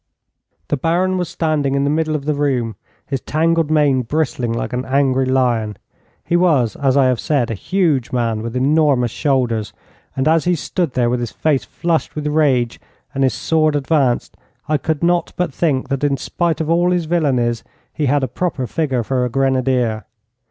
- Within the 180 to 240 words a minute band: Yes, average, 190 wpm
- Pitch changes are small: No, average, 3.9 semitones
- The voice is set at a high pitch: No, medium, 140 Hz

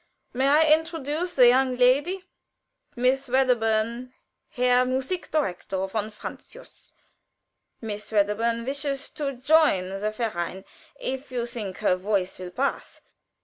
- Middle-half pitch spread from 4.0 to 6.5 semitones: Yes, average, 4.4 semitones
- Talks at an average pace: No, slow, 120 wpm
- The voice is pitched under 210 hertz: No, very high, 250 Hz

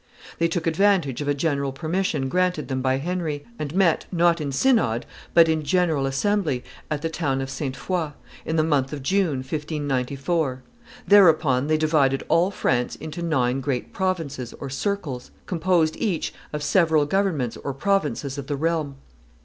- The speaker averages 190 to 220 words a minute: No, average, 165 wpm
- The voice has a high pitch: No, medium, 155 Hz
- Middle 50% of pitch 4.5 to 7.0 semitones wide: No, average, 4.1 semitones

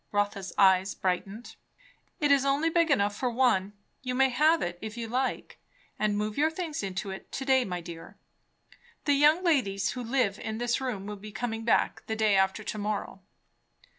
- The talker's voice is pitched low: No, high, 220 Hz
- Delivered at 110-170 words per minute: No, average, 190 wpm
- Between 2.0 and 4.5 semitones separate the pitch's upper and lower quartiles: No, average, 5.1 semitones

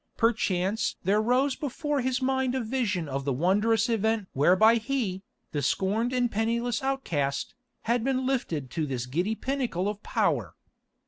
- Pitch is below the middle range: No, high, 225 Hz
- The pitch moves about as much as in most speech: No, wide, 5.7 semitones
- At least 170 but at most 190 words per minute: No, average, 150 wpm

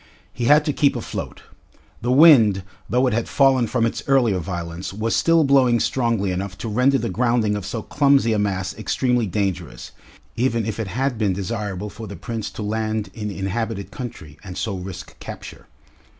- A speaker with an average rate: Yes, average, 180 wpm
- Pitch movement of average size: Yes, average, 4.0 semitones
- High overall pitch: No, low, 110 Hz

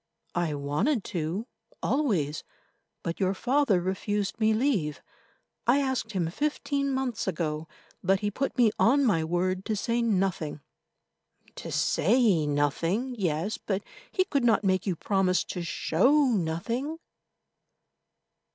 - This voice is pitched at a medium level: No, high, 195 Hz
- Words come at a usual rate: No, slow, 125 wpm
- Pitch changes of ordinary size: No, wide, 6.3 semitones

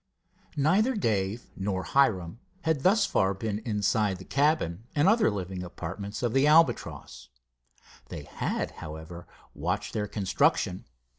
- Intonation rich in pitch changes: Yes, wide, 7.5 semitones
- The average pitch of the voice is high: No, low, 105 Hz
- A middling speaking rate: No, slow, 130 wpm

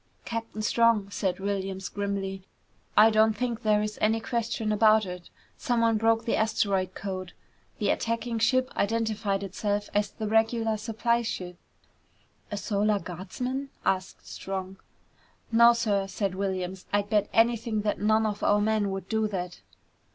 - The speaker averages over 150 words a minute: No, average, 145 wpm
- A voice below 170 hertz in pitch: No, high, 210 Hz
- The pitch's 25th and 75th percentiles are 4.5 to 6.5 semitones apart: No, narrow, 2.4 semitones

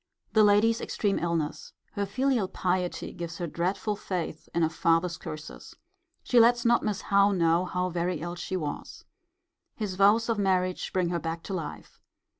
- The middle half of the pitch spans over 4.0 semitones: No, average, 3.3 semitones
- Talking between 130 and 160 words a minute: No, average, 170 wpm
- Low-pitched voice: No, medium, 185 Hz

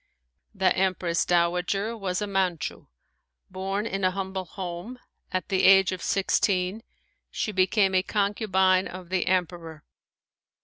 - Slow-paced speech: Yes, slow, 130 wpm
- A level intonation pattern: Yes, narrow, 1.4 semitones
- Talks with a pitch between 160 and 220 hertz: Yes, high, 190 Hz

